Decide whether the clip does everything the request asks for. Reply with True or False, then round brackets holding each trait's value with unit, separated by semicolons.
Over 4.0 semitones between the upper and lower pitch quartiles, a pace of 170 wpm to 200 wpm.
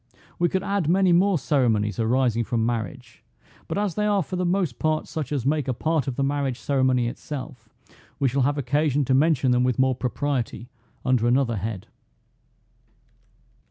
True (4.4 semitones; 175 wpm)